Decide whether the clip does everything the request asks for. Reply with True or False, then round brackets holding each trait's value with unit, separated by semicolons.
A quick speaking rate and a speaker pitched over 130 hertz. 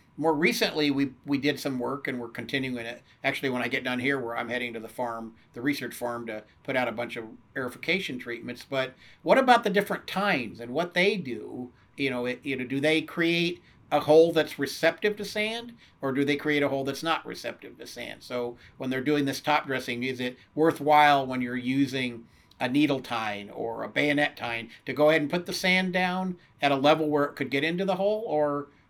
True (225 wpm; 140 Hz)